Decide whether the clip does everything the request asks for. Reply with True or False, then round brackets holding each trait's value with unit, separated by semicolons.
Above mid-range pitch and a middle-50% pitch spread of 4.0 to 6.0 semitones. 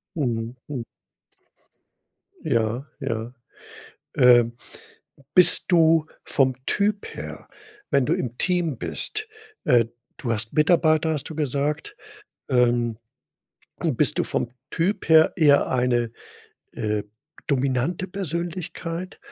False (140 Hz; 5.4 semitones)